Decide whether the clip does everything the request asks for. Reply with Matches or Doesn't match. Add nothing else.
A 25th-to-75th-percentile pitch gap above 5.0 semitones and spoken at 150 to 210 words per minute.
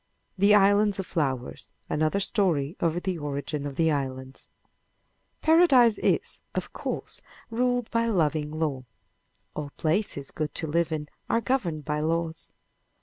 Doesn't match